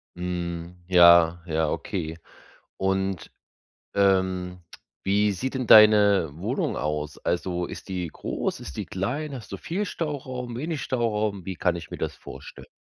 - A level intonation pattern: No, average, 4.0 semitones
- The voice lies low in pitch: Yes, very low, 95 Hz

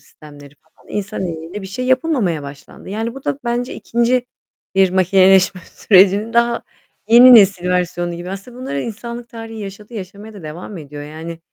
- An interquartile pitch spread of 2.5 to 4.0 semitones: No, average, 5.1 semitones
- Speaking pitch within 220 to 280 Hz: No, high, 195 Hz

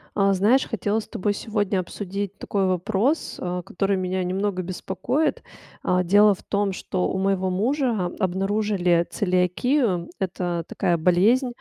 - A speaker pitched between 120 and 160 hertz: No, high, 195 Hz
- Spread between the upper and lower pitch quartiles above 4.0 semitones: No, narrow, 2.5 semitones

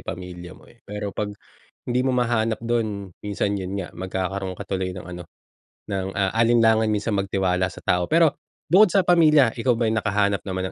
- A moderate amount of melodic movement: Yes, average, 3.8 semitones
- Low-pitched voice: Yes, low, 105 Hz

